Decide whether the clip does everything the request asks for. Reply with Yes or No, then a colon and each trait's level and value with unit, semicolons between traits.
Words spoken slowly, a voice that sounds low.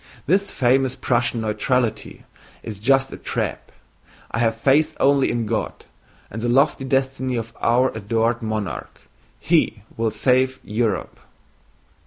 Yes: slow, 130 wpm; low, 120 Hz